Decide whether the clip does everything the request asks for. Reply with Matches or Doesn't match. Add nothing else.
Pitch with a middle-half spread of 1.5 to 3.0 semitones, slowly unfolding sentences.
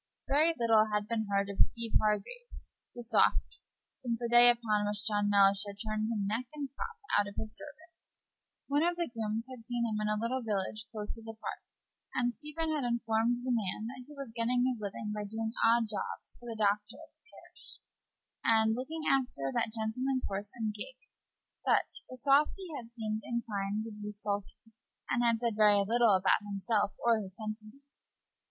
Doesn't match